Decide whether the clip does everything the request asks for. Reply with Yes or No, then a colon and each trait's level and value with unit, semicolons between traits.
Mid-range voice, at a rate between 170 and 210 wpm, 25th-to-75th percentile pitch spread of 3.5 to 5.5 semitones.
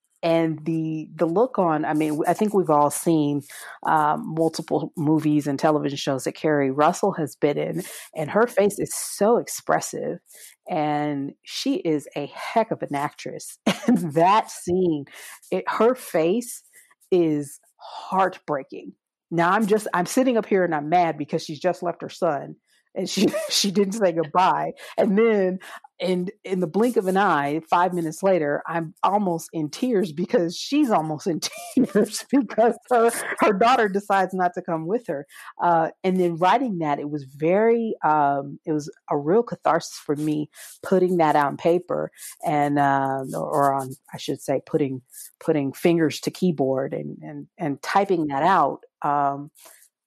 No: medium, 170 Hz; average, 160 wpm; average, 4.6 semitones